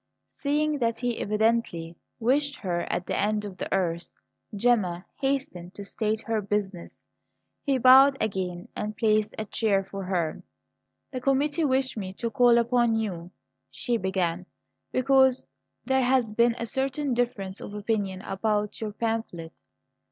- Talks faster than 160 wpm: No, average, 145 wpm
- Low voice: No, high, 220 Hz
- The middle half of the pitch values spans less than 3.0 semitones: No, average, 4.6 semitones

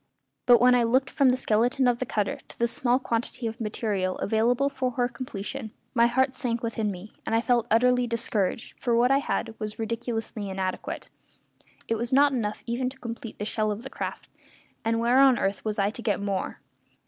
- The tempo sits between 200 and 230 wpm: Yes, fast, 205 wpm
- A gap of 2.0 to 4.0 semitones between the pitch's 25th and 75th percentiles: Yes, narrow, 2.6 semitones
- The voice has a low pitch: No, high, 235 Hz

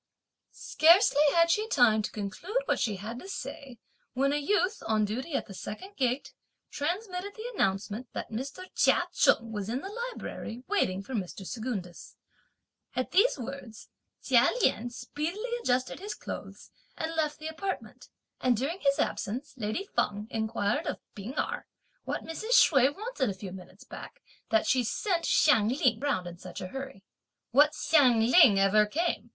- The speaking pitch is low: No, very high, 260 Hz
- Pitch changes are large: Yes, wide, 7.7 semitones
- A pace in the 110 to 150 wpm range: No, average, 165 wpm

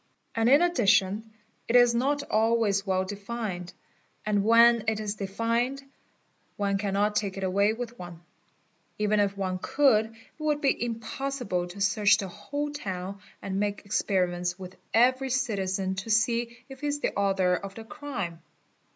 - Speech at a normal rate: Yes, average, 160 wpm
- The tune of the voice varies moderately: Yes, average, 3.5 semitones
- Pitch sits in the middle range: No, high, 210 Hz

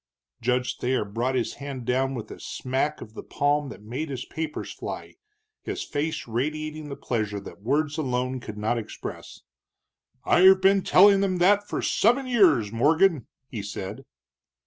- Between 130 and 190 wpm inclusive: Yes, average, 160 wpm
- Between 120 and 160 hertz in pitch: Yes, low, 135 Hz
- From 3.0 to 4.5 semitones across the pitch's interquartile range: No, average, 4.9 semitones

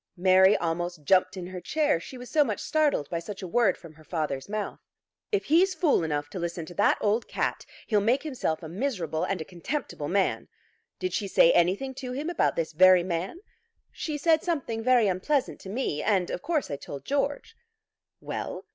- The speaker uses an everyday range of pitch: No, wide, 8.0 semitones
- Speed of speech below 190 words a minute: No, average, 200 wpm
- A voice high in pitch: Yes, high, 195 Hz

